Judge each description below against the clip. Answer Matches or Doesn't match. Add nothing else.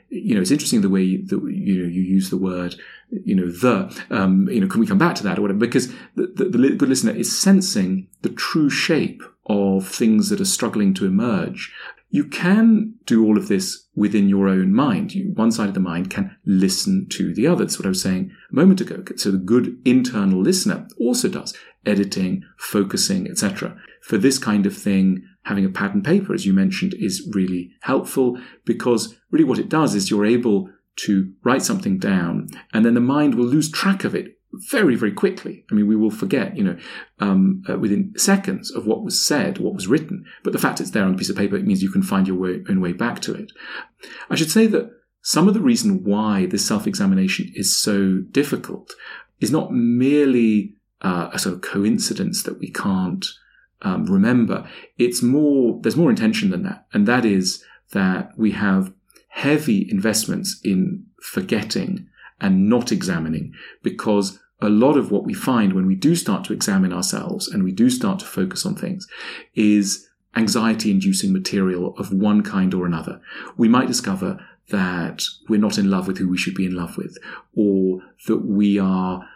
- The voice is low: Doesn't match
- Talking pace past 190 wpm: Matches